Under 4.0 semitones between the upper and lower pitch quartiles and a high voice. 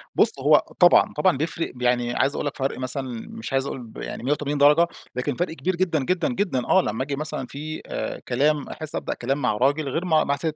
No: average, 3.4 semitones; medium, 140 Hz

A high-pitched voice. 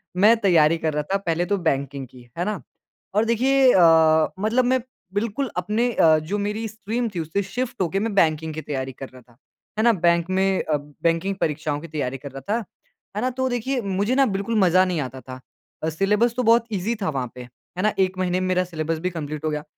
No: medium, 180 Hz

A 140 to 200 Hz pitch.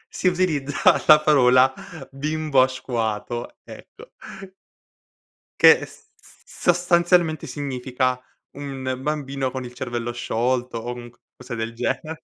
No: low, 130 Hz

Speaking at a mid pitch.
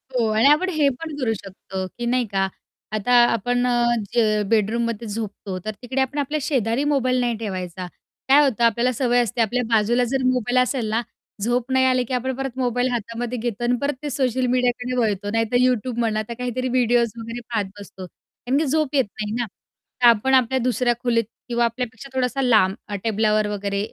No: high, 240 Hz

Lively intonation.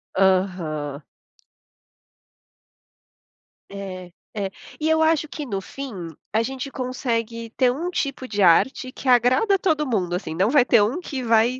Yes: wide, 5.8 semitones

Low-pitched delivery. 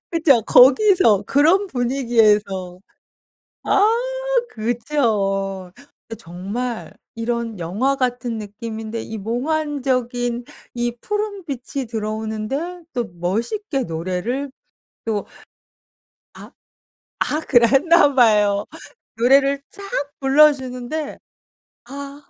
No: high, 240 Hz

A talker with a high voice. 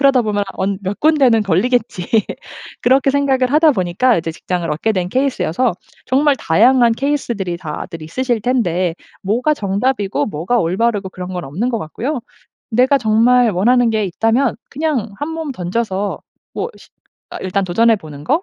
Yes: high, 225 Hz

